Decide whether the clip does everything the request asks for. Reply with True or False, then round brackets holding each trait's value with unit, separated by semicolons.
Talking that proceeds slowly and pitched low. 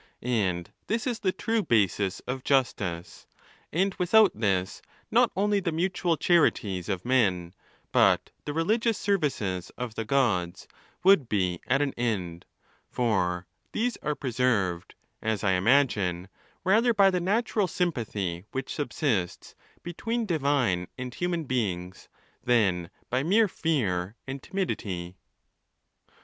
True (125 wpm; 125 Hz)